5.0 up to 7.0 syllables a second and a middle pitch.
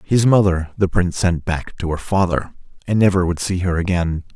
No: 5.3 syllables/s; very low, 90 Hz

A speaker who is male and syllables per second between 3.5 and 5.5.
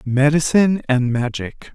Yes: male; 4.5 syllables/s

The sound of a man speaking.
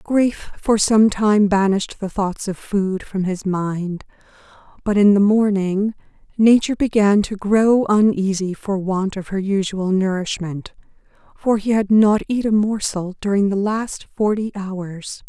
No: female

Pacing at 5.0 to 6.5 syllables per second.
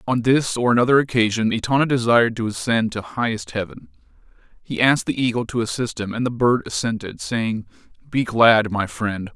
Yes: 5.5 syllables/s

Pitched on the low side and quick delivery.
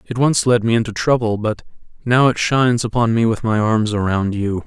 Yes: low, 115 Hz; fast, 220 wpm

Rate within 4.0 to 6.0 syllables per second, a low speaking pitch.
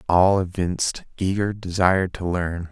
Yes: 4.6 syllables/s; very low, 90 Hz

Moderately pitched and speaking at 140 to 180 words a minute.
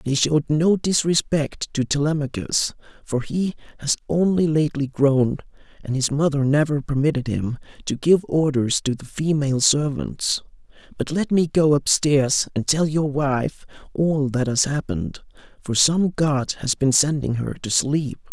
Yes: medium, 145 Hz; average, 155 wpm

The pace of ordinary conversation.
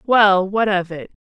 Yes: average, 195 wpm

